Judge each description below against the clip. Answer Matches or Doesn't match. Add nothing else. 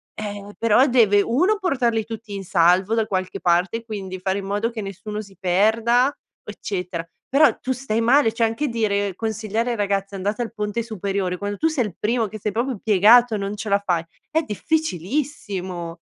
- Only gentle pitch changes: Doesn't match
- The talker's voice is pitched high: Matches